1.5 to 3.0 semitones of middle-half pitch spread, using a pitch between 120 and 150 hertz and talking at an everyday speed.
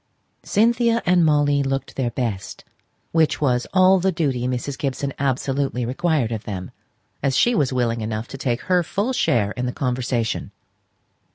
No: average, 5.0 semitones; low, 135 Hz; average, 160 wpm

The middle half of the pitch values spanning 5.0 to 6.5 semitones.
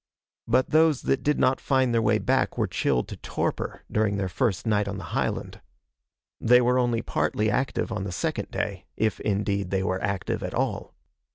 No: average, 4.0 semitones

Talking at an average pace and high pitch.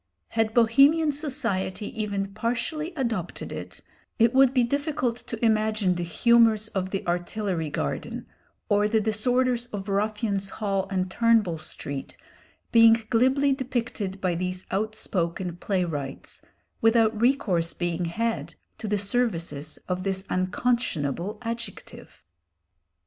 No: slow, 120 wpm; high, 215 Hz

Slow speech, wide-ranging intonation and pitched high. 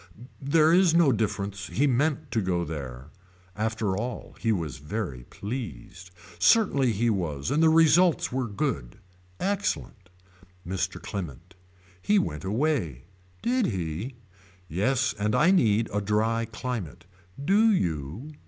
No: slow, 130 wpm; wide, 8.1 semitones; low, 110 Hz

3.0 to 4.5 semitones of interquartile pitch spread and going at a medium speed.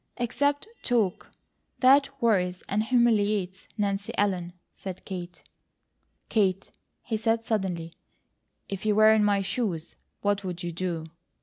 No: average, 3.5 semitones; slow, 125 wpm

